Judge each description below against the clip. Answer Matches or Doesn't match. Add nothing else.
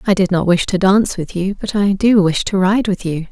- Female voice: Matches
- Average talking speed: Doesn't match